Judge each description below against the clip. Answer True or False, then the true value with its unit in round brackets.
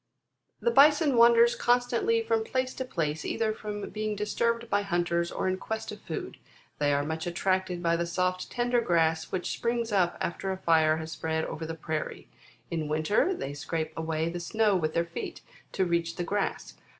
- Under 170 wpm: False (190 wpm)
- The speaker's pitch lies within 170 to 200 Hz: True (185 Hz)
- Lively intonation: True (6.1 semitones)